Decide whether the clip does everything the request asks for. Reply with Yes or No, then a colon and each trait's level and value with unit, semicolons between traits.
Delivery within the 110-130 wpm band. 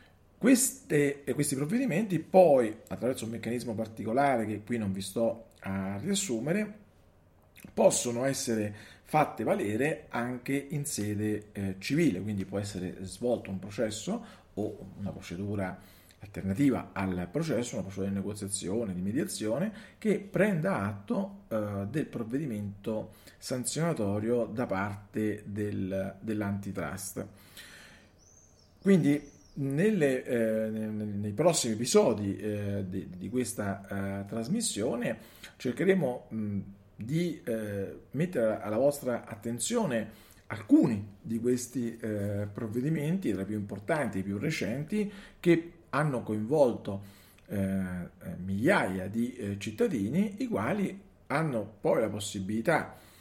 Yes: slow, 115 wpm